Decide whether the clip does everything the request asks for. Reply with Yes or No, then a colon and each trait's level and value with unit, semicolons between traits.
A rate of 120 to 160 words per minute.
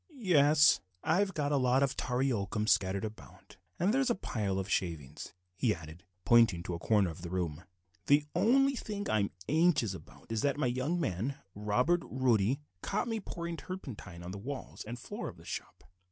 No: average, 190 wpm